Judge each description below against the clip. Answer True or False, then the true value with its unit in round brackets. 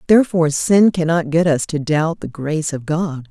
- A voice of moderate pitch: True (160 Hz)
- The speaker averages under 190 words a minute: False (200 wpm)